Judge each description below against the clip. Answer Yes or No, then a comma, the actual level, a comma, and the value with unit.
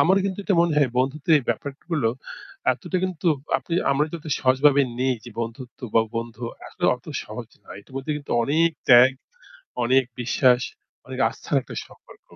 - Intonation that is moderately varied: Yes, average, 3.9 semitones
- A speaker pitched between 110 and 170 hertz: Yes, low, 135 Hz